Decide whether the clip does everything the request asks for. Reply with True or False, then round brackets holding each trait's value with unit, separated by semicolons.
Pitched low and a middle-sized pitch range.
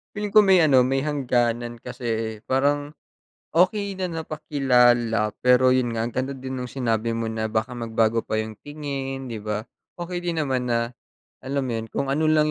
True (130 Hz; 3.9 semitones)